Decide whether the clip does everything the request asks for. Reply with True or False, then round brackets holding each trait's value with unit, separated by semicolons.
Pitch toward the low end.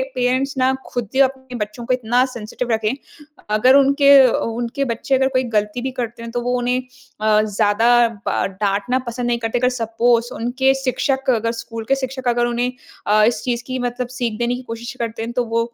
False (240 Hz)